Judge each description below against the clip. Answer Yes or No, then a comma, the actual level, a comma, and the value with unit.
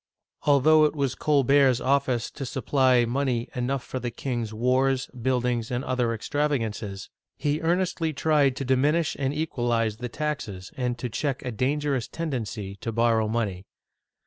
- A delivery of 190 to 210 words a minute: No, average, 145 wpm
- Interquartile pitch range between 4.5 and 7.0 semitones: No, average, 3.3 semitones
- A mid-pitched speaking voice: No, low, 130 Hz